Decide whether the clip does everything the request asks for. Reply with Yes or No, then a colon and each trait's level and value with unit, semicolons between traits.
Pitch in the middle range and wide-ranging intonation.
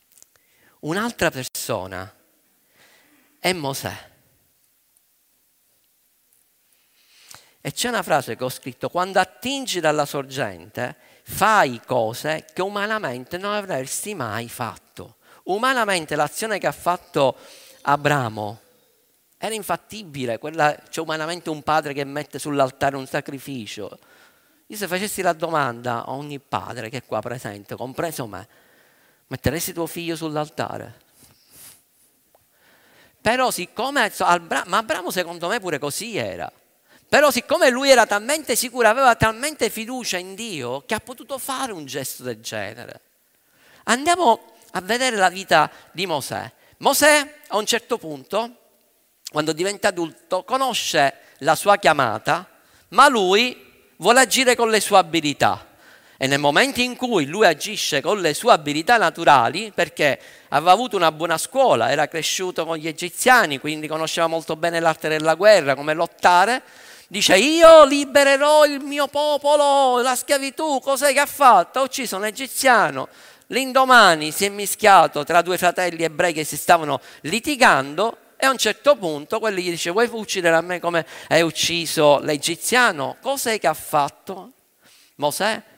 Yes: medium, 180 Hz; wide, 7.8 semitones